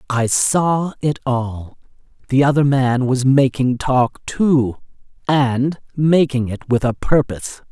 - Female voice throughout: No, male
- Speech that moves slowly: Yes, slow, 130 wpm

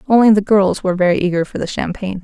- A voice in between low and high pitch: No, high, 195 Hz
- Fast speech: Yes, fast, 240 wpm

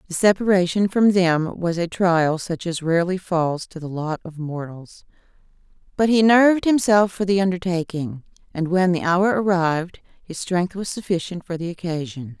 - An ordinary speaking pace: Yes, average, 170 wpm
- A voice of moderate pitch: Yes, medium, 175 Hz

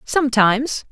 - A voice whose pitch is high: Yes, very high, 250 Hz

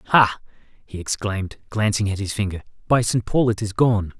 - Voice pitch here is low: Yes, low, 105 Hz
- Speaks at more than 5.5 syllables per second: No, 4.9 syllables/s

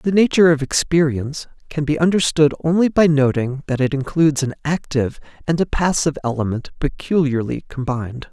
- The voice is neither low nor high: Yes, medium, 150 Hz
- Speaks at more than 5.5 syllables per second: Yes, 5.8 syllables/s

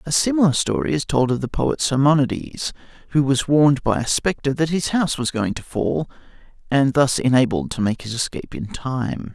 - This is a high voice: No, medium, 140 Hz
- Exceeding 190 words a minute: Yes, average, 200 wpm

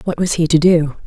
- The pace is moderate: No, fast, 280 wpm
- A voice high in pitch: No, medium, 165 Hz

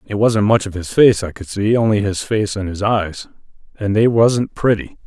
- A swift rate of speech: Yes, fast, 215 wpm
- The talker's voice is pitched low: Yes, low, 105 Hz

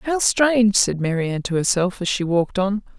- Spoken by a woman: Yes, female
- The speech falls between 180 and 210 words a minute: Yes, average, 200 wpm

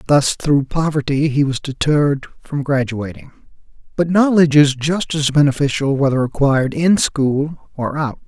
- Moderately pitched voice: Yes, medium, 145 Hz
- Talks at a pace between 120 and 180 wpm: Yes, average, 145 wpm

